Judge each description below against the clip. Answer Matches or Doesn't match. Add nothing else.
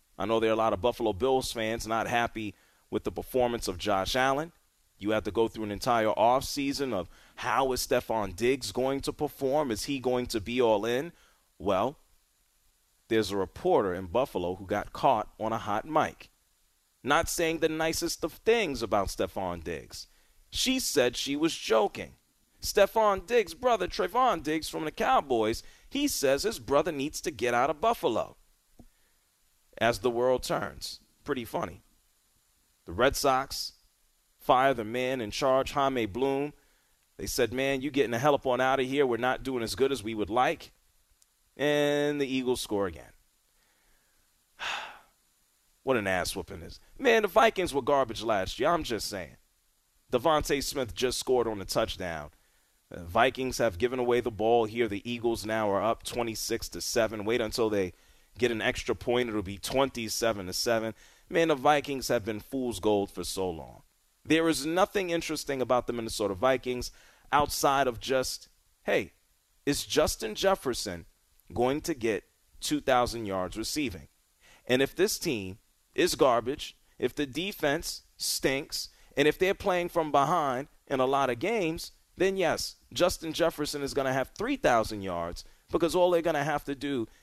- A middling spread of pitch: Matches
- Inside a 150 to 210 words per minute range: Matches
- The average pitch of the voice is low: Matches